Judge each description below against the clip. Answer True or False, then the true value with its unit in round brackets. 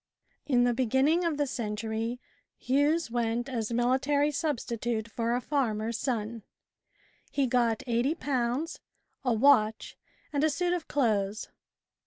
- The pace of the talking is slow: True (125 wpm)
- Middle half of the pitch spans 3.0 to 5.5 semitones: True (3.9 semitones)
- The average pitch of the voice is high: True (245 Hz)